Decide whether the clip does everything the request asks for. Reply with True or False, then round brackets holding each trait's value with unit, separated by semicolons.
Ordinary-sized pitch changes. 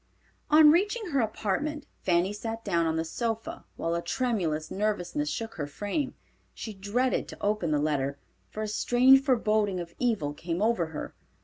False (6.5 semitones)